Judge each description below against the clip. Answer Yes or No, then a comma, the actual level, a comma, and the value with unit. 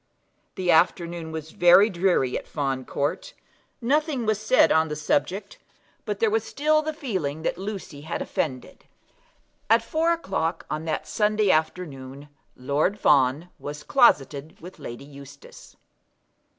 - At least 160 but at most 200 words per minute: No, average, 140 wpm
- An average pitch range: No, wide, 6.9 semitones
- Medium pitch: Yes, medium, 170 Hz